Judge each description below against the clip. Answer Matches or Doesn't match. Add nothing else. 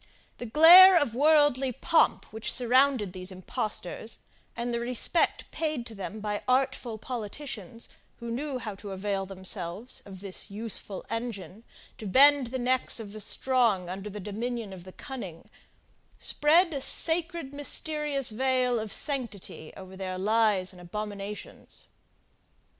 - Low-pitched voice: Doesn't match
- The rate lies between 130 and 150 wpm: Matches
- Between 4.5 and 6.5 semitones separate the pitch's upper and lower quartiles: Matches